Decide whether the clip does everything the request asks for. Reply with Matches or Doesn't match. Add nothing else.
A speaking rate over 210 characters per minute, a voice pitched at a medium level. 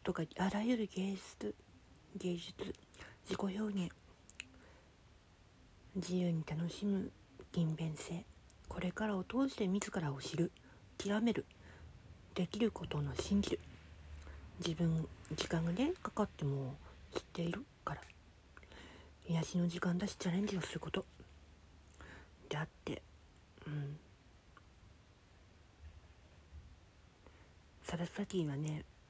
Doesn't match